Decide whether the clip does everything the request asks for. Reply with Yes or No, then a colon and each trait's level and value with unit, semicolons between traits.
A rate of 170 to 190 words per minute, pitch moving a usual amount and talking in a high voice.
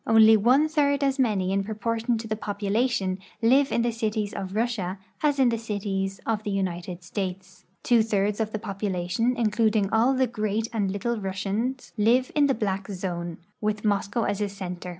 Yes: average, 180 wpm; average, 3.1 semitones; high, 215 Hz